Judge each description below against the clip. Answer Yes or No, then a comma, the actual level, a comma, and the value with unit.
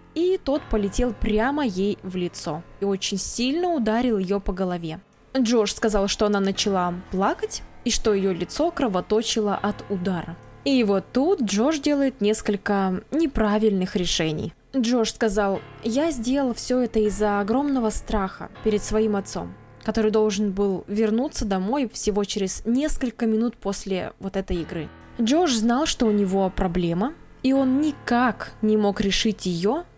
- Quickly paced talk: No, average, 145 wpm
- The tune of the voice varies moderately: Yes, average, 4.0 semitones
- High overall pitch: Yes, high, 215 Hz